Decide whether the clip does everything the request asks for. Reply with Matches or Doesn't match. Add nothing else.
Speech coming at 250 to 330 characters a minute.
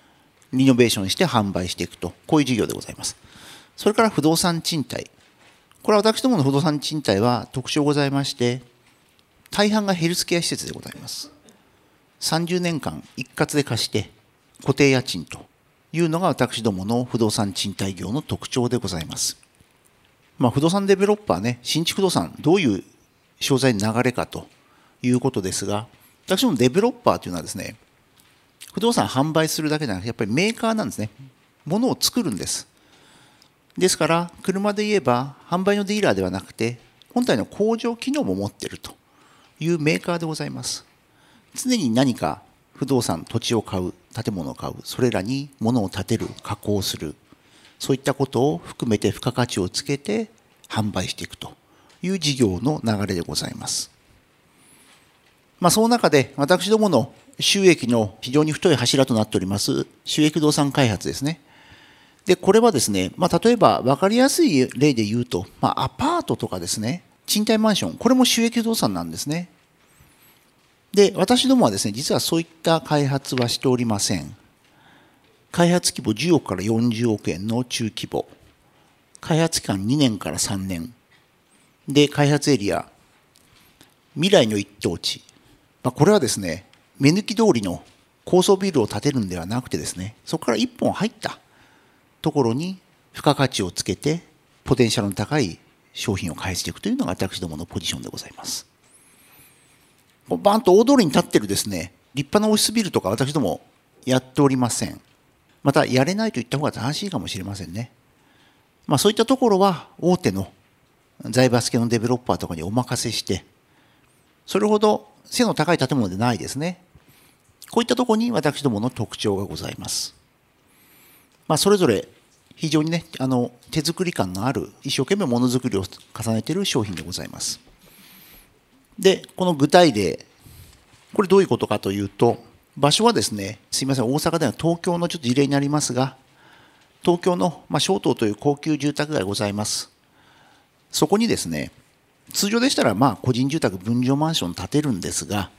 Doesn't match